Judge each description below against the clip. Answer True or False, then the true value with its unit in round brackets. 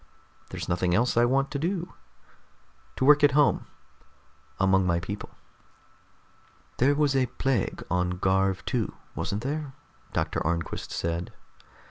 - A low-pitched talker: True (120 Hz)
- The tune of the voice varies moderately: False (7.5 semitones)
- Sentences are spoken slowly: True (130 wpm)